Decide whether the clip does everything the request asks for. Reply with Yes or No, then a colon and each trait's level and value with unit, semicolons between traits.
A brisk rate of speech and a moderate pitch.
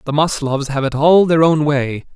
Yes: fast, 225 wpm; medium, 145 Hz